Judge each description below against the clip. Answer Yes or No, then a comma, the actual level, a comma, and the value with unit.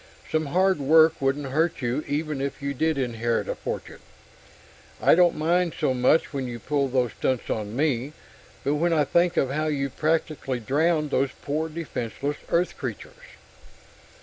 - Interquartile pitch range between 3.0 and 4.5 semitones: Yes, average, 3.3 semitones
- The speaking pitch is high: No, medium, 145 Hz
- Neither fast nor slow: Yes, average, 165 wpm